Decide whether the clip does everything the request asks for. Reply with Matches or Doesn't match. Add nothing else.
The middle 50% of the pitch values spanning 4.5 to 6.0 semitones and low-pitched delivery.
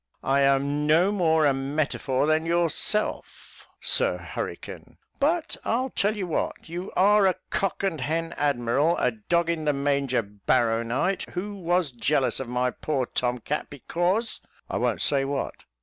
Doesn't match